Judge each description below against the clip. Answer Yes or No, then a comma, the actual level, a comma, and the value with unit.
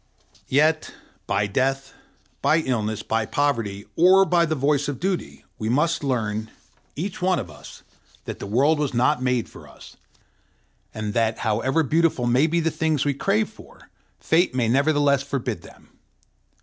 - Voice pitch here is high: No, medium, 140 Hz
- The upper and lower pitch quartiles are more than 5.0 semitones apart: Yes, wide, 5.5 semitones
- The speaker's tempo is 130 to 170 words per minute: Yes, average, 160 wpm